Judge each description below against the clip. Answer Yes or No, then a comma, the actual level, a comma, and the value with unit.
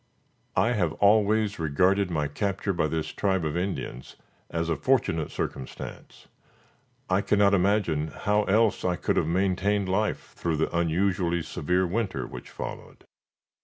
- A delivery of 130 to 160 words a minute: Yes, average, 140 wpm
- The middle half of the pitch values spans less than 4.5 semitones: Yes, average, 3.7 semitones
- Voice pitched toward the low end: Yes, very low, 95 Hz